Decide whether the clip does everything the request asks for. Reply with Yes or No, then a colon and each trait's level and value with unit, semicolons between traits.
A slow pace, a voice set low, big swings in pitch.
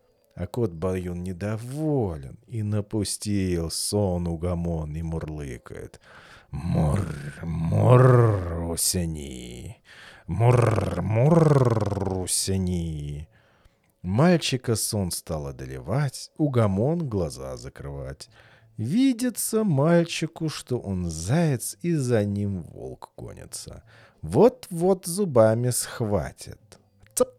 Yes: slow, 80 wpm; low, 105 Hz; wide, 7.4 semitones